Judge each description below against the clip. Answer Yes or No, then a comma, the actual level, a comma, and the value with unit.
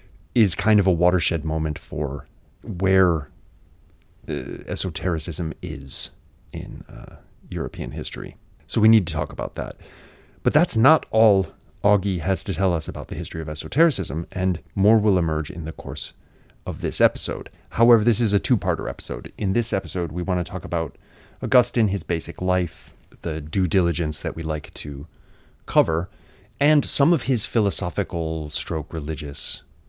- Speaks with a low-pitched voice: Yes, very low, 90 Hz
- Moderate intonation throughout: Yes, average, 4.1 semitones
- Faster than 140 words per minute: Yes, average, 160 wpm